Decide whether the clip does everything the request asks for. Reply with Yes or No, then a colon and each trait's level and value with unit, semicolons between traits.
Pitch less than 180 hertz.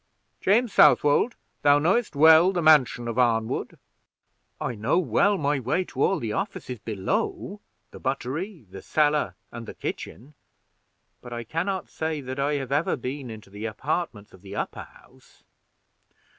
Yes: medium, 140 Hz